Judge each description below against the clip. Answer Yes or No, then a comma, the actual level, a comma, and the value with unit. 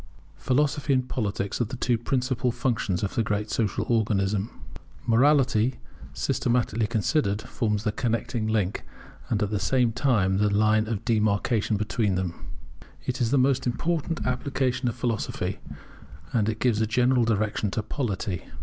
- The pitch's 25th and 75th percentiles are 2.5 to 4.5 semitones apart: Yes, average, 3.2 semitones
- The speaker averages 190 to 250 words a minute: No, average, 150 wpm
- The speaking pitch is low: Yes, low, 115 Hz